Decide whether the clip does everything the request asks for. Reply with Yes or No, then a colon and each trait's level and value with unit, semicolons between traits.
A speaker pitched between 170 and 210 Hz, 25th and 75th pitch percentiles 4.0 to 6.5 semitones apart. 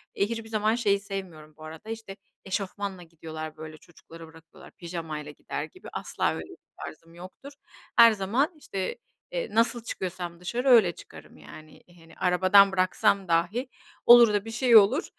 Yes: high, 190 Hz; average, 5.2 semitones